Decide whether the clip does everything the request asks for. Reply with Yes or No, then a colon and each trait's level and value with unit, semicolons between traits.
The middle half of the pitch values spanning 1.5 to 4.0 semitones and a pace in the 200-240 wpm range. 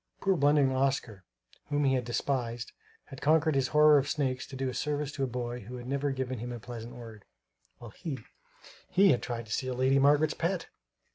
Yes: average, 3.1 semitones; fast, 205 wpm